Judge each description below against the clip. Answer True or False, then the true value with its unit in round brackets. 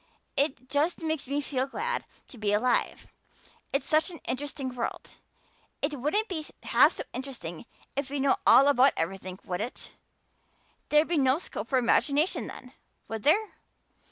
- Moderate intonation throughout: True (3.4 semitones)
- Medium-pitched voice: False (275 Hz)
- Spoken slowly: False (155 wpm)